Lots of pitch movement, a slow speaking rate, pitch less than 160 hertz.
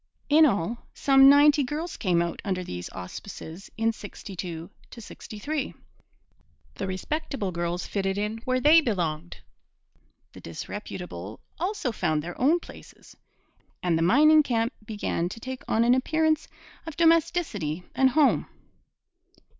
No: wide, 8.5 semitones; slow, 130 wpm; high, 225 Hz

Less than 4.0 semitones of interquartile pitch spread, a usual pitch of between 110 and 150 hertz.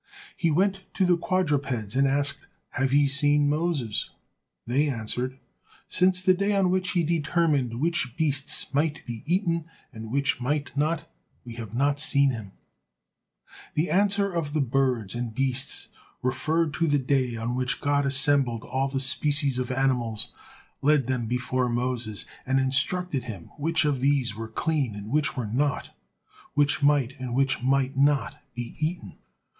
Yes: average, 3.5 semitones; medium, 140 Hz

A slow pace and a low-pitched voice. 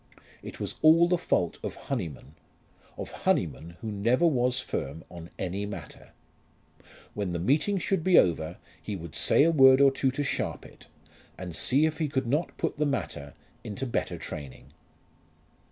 No: average, 165 wpm; low, 125 Hz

